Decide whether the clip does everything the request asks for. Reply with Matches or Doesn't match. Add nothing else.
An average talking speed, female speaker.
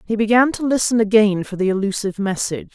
Matches